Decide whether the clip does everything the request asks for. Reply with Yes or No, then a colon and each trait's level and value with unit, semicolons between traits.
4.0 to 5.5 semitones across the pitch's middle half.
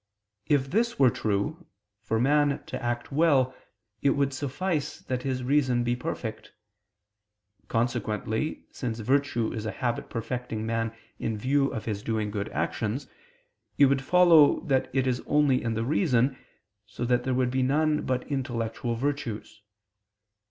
No: average, 3.6 semitones